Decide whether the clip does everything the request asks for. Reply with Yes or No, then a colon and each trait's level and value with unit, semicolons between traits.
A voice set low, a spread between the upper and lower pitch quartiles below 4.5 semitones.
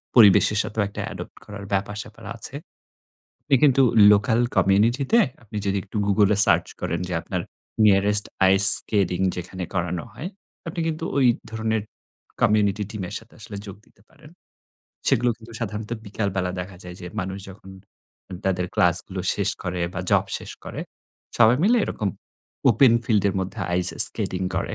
Yes: low, 100 Hz; average, 2.9 semitones